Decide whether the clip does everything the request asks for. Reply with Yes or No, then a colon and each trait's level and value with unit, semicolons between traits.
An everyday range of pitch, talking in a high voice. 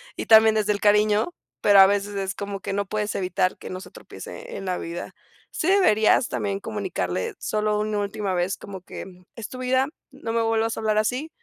No: narrow, 2.2 semitones; high, 210 Hz